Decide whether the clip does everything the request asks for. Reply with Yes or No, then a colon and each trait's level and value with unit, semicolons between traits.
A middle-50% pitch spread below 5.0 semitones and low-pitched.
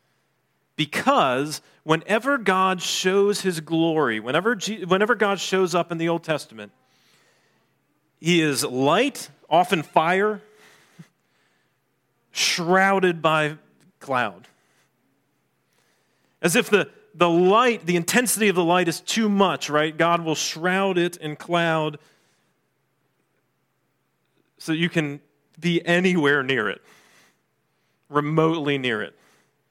No: average, 3.6 semitones; medium, 170 Hz